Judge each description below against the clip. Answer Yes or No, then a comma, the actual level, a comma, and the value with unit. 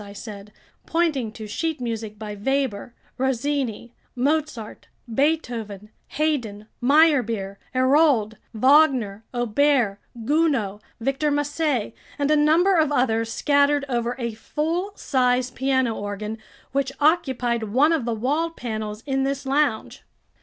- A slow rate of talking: Yes, slow, 120 wpm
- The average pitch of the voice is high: Yes, very high, 255 Hz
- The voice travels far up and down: No, average, 4.8 semitones